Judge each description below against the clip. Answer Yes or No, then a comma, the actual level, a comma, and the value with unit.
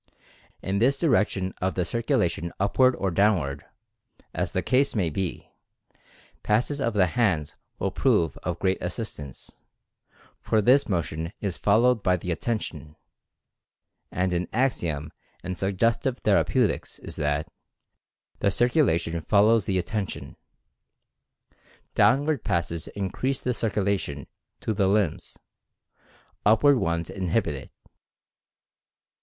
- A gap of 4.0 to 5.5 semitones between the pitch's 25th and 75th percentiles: Yes, average, 5.1 semitones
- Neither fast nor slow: No, slow, 125 wpm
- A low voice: Yes, low, 100 Hz